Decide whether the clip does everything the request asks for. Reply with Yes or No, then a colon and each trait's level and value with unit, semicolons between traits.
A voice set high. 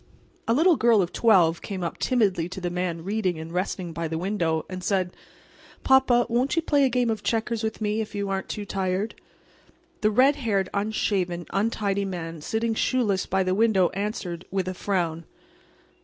Yes: high, 200 Hz